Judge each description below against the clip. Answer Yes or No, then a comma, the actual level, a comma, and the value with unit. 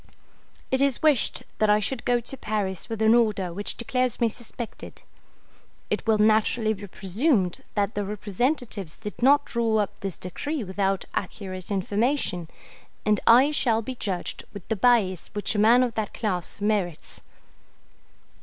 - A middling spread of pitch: Yes, average, 3.5 semitones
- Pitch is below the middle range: No, high, 215 Hz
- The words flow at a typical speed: Yes, average, 155 wpm